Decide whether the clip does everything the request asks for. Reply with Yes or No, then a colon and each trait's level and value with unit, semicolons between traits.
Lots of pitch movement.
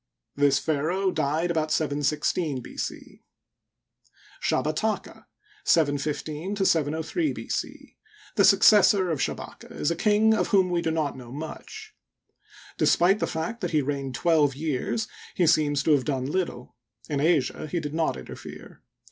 No: average, 4.1 semitones